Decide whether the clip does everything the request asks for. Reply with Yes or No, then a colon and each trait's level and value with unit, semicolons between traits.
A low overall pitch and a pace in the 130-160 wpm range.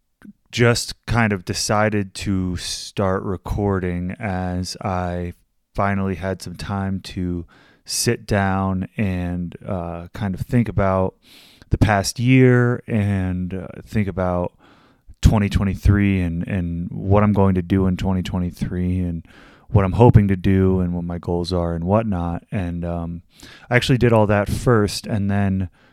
Yes: very low, 95 Hz; average, 145 wpm